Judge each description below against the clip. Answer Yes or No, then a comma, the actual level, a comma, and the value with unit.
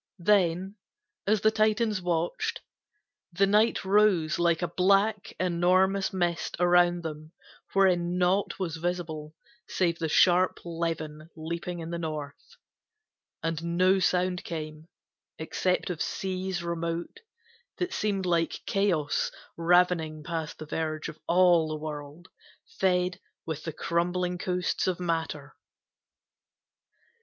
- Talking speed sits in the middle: No, slow, 120 wpm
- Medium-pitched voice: Yes, medium, 175 Hz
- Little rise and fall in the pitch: Yes, narrow, 2.3 semitones